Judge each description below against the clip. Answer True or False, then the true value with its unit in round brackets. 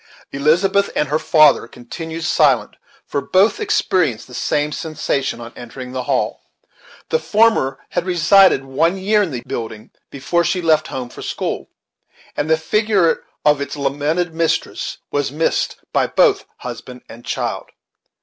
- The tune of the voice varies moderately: True (4.7 semitones)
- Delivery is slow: False (150 wpm)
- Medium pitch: True (155 Hz)